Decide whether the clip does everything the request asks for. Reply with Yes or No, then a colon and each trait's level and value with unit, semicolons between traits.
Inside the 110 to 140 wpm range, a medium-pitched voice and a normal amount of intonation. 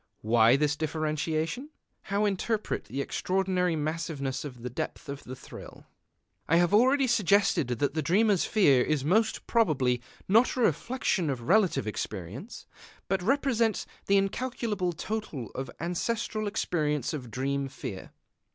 No: slow, 135 wpm; medium, 165 Hz; wide, 7.3 semitones